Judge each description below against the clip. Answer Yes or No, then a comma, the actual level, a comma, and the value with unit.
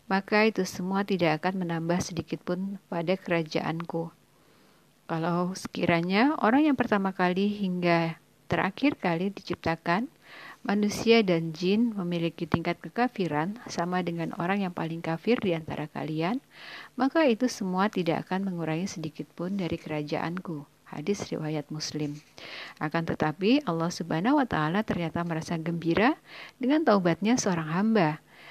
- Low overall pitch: No, medium, 180 Hz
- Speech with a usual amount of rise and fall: Yes, average, 3.7 semitones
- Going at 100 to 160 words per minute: Yes, average, 130 wpm